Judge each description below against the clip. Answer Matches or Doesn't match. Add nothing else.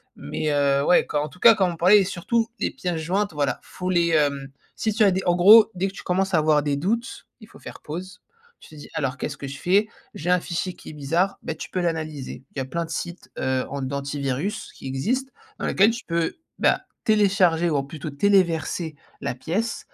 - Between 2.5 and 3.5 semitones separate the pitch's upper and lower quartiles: Doesn't match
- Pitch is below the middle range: Doesn't match